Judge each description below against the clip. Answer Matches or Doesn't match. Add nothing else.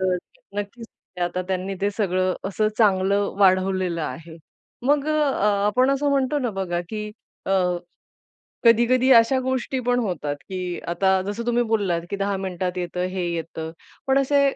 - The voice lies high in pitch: Matches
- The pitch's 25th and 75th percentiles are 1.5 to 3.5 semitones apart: Doesn't match